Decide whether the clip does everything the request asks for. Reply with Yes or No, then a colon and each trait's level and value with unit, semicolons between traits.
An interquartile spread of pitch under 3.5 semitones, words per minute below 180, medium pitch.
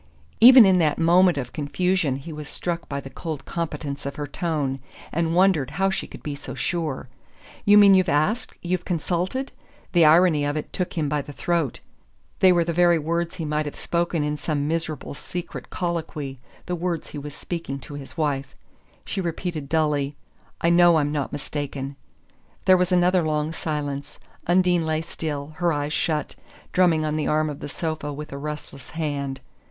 No: average, 3.1 semitones; average, 185 wpm; medium, 155 Hz